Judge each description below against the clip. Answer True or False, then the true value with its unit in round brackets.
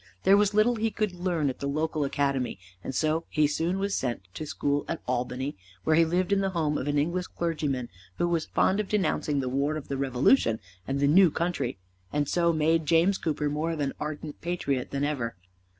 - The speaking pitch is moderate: True (155 Hz)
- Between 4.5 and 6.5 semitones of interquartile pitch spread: False (3.7 semitones)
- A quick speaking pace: True (215 wpm)